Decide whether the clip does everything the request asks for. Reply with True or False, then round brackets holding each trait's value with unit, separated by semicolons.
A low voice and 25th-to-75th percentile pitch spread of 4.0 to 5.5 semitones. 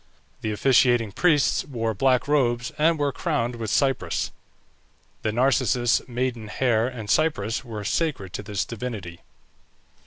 False (120 Hz; 3.6 semitones)